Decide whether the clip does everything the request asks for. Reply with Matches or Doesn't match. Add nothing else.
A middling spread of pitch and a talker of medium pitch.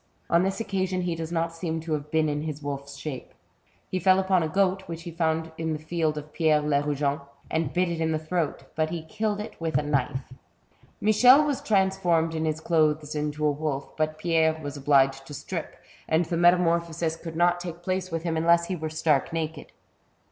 Doesn't match